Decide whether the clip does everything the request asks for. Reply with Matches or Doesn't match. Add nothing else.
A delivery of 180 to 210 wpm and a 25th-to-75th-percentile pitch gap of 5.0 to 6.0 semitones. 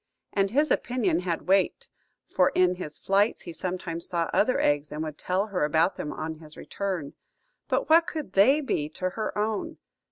Doesn't match